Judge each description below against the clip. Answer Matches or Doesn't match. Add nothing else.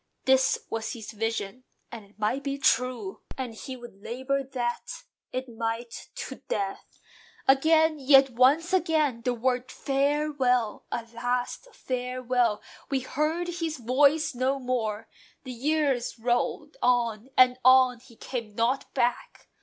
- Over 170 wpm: Doesn't match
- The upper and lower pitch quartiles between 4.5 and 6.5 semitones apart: Doesn't match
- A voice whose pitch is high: Matches